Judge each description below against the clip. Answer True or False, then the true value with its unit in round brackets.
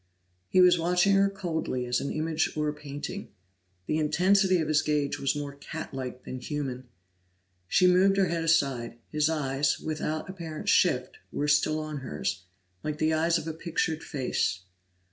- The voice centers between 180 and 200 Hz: False (155 Hz)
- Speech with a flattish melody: False (3.1 semitones)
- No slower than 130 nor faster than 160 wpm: False (170 wpm)